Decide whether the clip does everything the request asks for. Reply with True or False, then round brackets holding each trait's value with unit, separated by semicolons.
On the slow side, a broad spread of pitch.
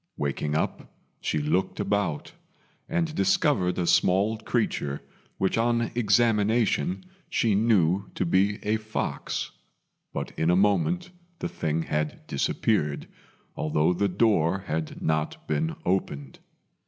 True (120 wpm; 5.7 semitones)